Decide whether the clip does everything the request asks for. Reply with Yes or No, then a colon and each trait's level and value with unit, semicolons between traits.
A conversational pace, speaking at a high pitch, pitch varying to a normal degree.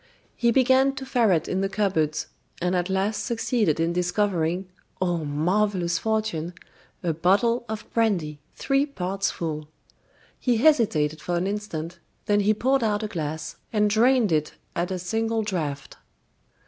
Yes: average, 150 wpm; high, 195 Hz; average, 4.7 semitones